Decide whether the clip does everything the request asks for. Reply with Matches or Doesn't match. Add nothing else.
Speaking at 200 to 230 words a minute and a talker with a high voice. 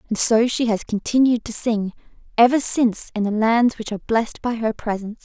Matches